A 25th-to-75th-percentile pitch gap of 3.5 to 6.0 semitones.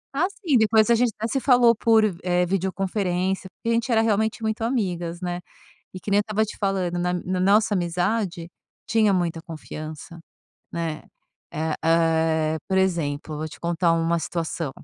Yes: average, 4.5 semitones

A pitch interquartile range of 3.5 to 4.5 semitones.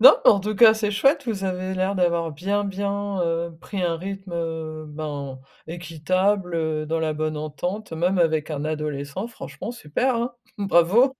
Yes: average, 4.2 semitones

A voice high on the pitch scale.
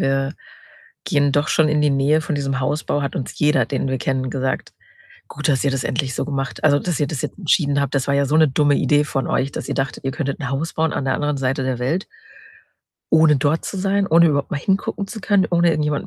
No: medium, 145 Hz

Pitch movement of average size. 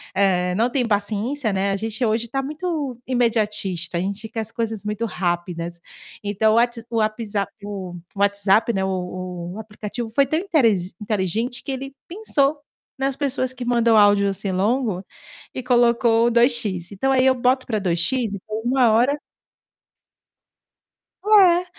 Yes: average, 4.0 semitones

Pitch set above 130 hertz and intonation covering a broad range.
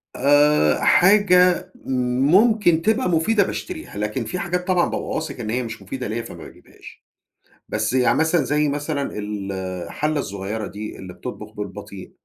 Yes: medium, 140 Hz; wide, 8.7 semitones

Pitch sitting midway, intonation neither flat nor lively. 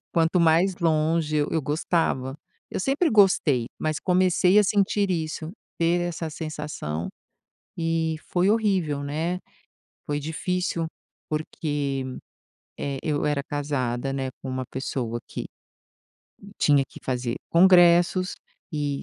Yes: medium, 160 Hz; average, 3.7 semitones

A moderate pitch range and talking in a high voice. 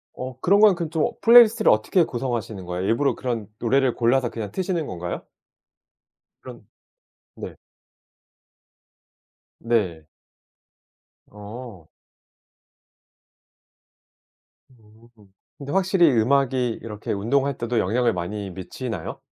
No: average, 4.8 semitones; low, 120 Hz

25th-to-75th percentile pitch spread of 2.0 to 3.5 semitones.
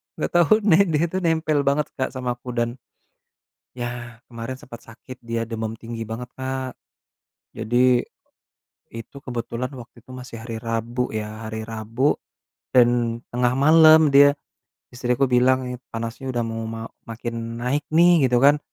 Yes: average, 2.7 semitones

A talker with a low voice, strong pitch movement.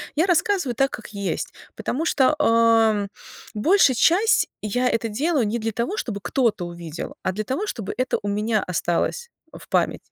No: high, 230 Hz; wide, 6.1 semitones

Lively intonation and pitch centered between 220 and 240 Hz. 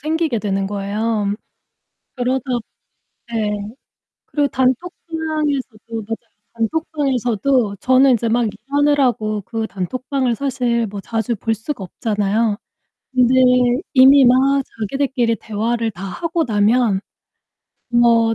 No: average, 3.8 semitones; high, 235 Hz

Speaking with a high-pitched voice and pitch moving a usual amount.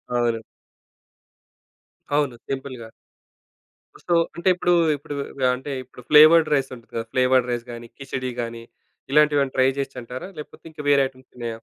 No: low, 130 Hz; average, 3.2 semitones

